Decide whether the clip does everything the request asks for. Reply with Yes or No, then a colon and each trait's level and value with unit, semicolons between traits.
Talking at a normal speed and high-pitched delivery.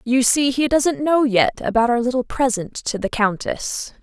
Yes: average, 195 wpm; very high, 250 Hz